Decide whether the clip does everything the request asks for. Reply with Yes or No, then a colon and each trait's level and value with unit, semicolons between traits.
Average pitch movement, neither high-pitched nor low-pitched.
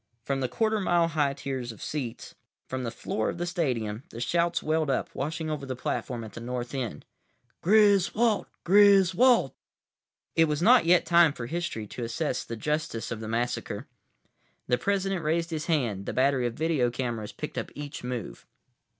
No: wide, 6.0 semitones; medium, 145 Hz